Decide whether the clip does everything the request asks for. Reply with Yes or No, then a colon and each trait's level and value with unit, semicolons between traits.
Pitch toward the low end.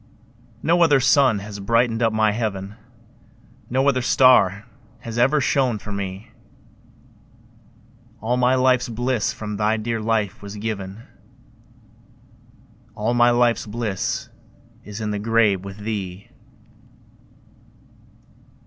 Yes: low, 110 Hz